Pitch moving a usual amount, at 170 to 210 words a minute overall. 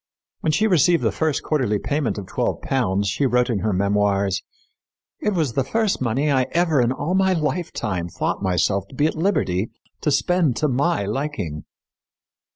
No: wide, 7.7 semitones; average, 175 wpm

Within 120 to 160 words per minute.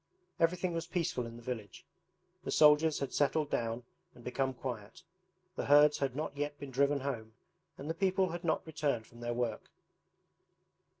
No: average, 170 wpm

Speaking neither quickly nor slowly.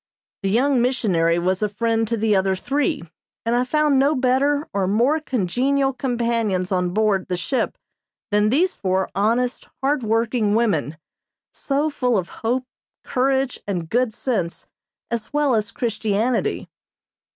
Yes: average, 145 wpm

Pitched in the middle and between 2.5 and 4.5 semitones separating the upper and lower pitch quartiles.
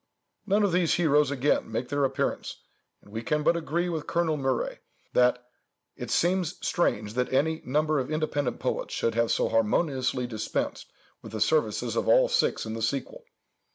No: medium, 145 Hz; average, 5.2 semitones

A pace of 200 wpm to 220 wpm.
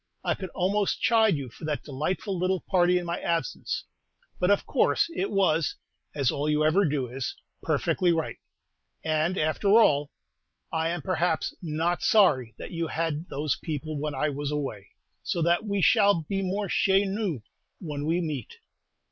No: average, 170 wpm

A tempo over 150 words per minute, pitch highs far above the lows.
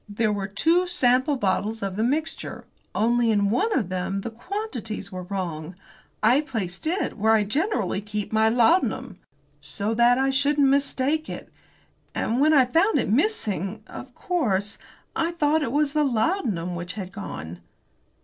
Yes: average, 160 wpm; wide, 6.5 semitones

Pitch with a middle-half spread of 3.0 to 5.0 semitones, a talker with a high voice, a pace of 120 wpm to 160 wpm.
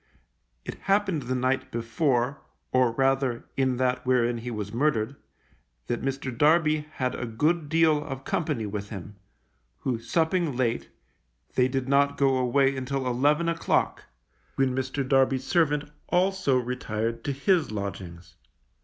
No: average, 3.4 semitones; low, 130 Hz; average, 140 wpm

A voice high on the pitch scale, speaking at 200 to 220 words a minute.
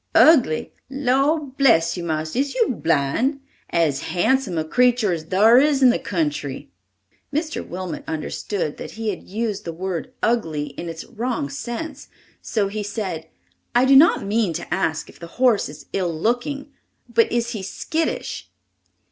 No: high, 210 Hz; average, 160 wpm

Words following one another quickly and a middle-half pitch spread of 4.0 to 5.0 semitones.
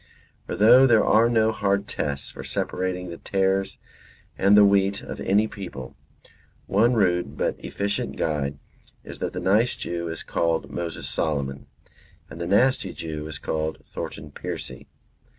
No: average, 150 wpm; average, 4.7 semitones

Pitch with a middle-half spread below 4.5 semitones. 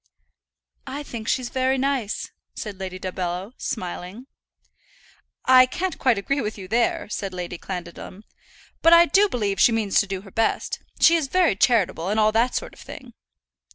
No: wide, 5.4 semitones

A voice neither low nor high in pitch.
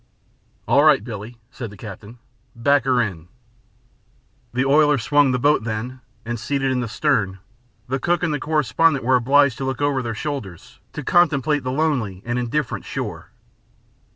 No: low, 130 Hz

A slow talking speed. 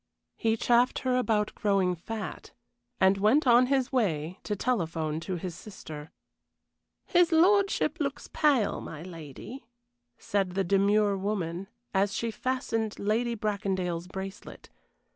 Yes: slow, 125 wpm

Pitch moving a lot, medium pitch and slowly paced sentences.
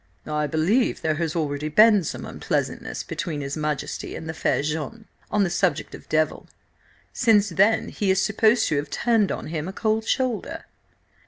No: wide, 5.8 semitones; medium, 175 Hz; average, 175 wpm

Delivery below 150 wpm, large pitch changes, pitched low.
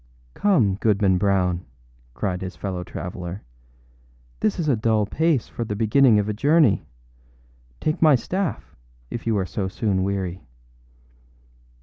No: slow, 135 wpm; average, 4.6 semitones; low, 105 Hz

